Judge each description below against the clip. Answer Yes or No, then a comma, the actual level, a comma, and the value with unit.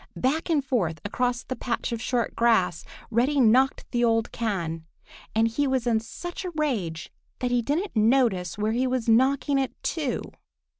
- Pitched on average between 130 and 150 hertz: No, high, 240 Hz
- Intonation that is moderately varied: Yes, average, 3.2 semitones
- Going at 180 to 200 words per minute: No, average, 170 wpm